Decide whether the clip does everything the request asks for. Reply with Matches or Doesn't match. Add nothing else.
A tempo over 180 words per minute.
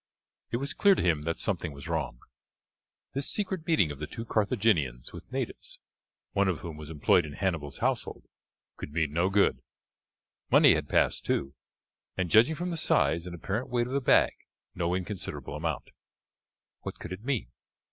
Doesn't match